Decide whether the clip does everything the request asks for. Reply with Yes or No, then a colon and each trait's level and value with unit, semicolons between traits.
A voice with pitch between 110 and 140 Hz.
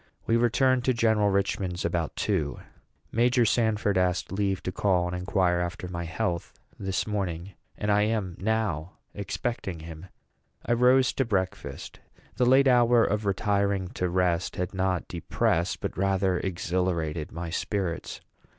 No: very low, 95 Hz